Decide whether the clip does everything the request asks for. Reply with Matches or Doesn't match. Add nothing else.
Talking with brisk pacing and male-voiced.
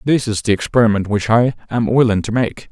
Matches